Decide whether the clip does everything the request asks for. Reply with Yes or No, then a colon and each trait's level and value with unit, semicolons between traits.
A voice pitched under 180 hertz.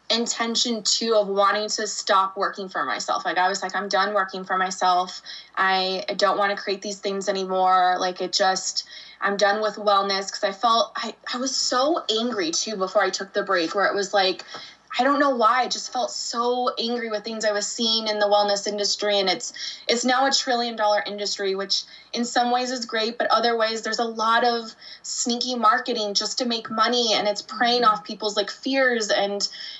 No: high, 210 Hz